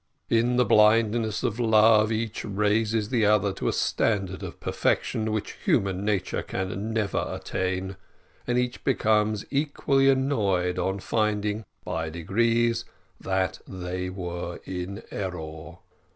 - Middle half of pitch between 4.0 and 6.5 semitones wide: No, average, 3.3 semitones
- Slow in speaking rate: Yes, slow, 125 wpm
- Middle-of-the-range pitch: No, low, 105 Hz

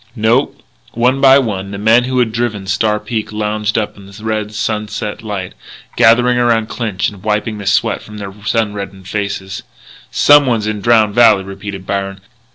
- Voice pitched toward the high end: No, low, 105 Hz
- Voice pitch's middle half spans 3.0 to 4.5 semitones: No, narrow, 2.4 semitones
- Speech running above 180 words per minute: No, average, 165 wpm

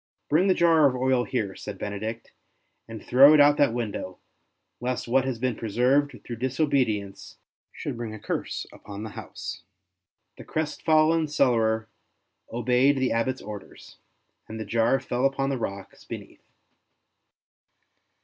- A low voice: Yes, low, 125 Hz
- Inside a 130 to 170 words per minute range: Yes, average, 155 wpm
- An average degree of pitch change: Yes, average, 3.8 semitones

